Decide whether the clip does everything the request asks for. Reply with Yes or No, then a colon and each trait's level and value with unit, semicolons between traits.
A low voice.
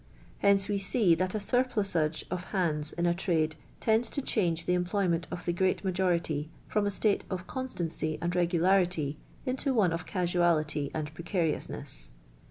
No: medium, 180 Hz